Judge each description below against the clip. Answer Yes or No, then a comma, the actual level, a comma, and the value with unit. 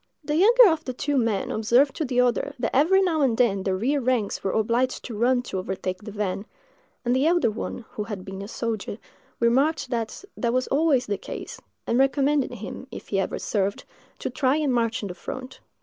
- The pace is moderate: No, fast, 210 wpm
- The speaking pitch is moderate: No, high, 245 Hz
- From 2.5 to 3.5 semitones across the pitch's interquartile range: No, average, 4.6 semitones